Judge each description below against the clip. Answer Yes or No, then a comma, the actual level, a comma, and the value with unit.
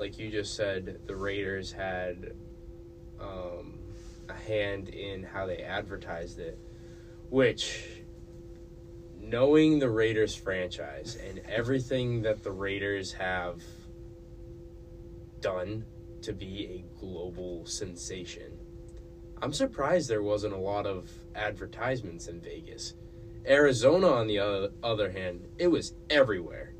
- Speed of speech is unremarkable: No, slow, 110 wpm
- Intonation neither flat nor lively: Yes, average, 4.7 semitones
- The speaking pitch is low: Yes, low, 100 Hz